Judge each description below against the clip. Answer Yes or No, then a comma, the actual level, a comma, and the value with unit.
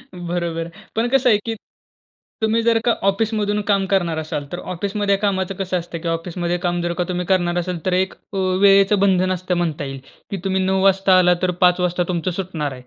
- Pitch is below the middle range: No, medium, 185 Hz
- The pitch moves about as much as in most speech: No, narrow, 2.1 semitones